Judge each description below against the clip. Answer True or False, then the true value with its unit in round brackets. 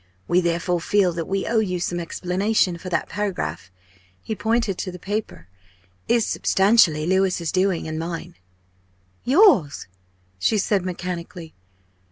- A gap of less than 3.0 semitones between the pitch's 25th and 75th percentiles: False (3.3 semitones)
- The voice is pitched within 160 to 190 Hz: True (185 Hz)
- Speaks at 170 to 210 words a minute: False (135 wpm)